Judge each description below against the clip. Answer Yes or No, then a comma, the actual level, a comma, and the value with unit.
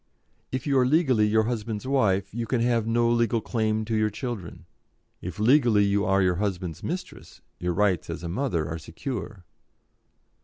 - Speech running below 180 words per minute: Yes, average, 165 wpm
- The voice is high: No, low, 110 Hz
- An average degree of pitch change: Yes, average, 3.8 semitones